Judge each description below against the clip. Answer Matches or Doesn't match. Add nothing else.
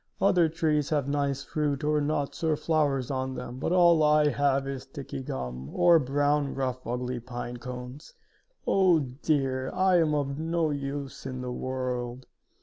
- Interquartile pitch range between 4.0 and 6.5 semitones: Doesn't match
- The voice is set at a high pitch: Doesn't match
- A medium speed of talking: Matches